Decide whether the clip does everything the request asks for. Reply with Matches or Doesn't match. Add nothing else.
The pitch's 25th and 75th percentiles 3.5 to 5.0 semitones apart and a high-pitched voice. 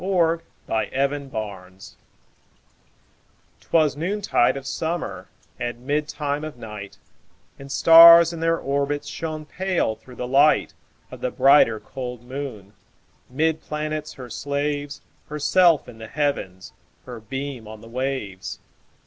Doesn't match